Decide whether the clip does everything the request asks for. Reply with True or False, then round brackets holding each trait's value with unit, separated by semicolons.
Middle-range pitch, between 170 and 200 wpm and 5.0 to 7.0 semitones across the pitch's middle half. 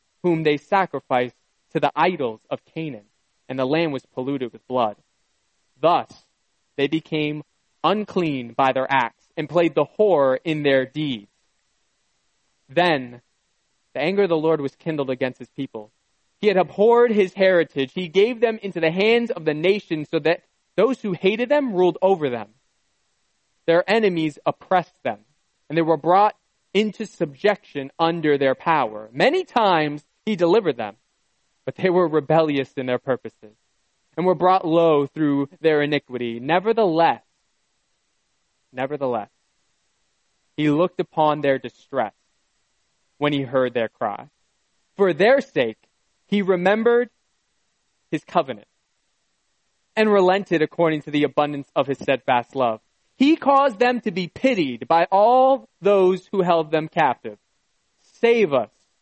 False (165 Hz; 140 wpm; 5.6 semitones)